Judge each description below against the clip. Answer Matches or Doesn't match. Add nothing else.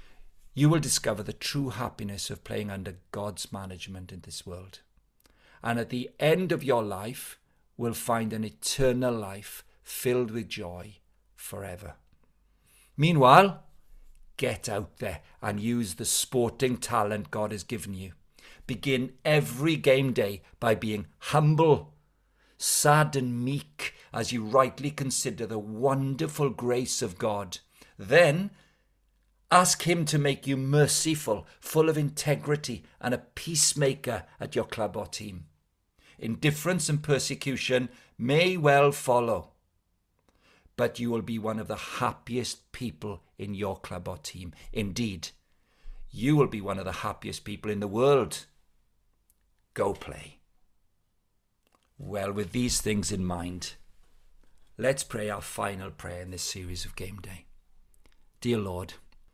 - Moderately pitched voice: Doesn't match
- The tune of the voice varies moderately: Doesn't match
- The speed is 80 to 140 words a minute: Matches